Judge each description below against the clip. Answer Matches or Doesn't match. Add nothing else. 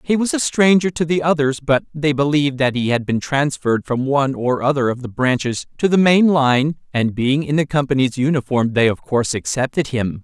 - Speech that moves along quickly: Matches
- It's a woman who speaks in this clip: Doesn't match